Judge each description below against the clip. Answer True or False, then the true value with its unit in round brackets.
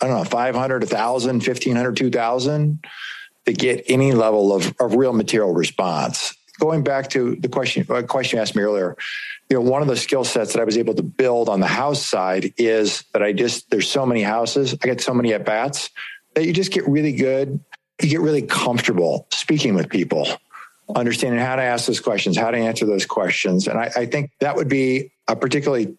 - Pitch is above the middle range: False (130 Hz)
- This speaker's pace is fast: True (210 wpm)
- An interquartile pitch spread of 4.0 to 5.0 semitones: True (4.4 semitones)